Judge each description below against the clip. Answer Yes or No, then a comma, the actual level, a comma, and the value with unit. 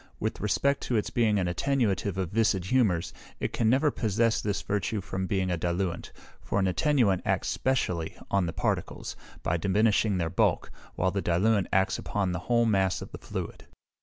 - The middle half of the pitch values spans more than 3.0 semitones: Yes, average, 3.5 semitones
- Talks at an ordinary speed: Yes, average, 185 wpm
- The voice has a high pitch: No, low, 100 Hz